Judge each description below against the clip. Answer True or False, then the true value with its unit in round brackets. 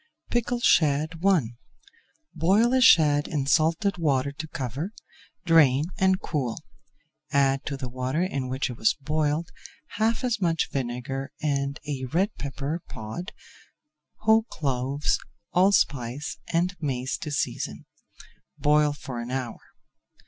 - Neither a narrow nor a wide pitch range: True (4.4 semitones)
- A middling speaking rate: False (125 wpm)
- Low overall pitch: False (145 Hz)